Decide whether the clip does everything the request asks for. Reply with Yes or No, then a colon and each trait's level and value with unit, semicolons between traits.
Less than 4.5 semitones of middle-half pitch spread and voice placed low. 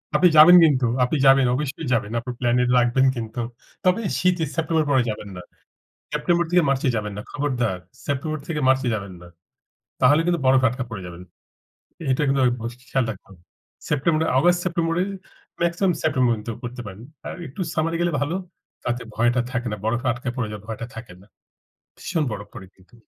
No: average, 5.2 semitones; low, 130 Hz